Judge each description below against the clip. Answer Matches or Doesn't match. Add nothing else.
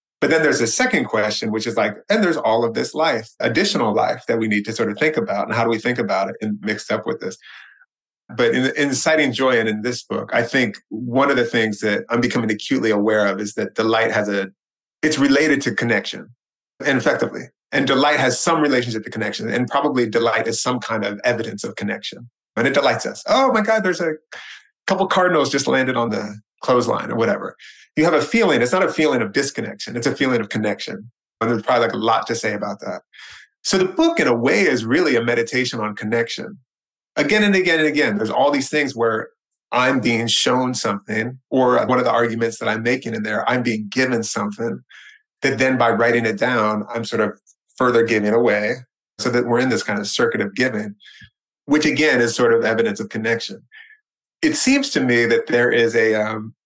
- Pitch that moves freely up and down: Doesn't match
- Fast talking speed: Matches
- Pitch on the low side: Matches